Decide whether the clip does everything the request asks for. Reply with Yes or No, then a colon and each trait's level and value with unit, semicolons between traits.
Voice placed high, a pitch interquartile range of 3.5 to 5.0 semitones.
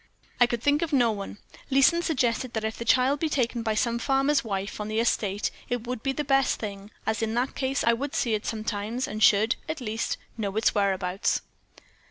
Yes: high, 235 Hz; average, 3.8 semitones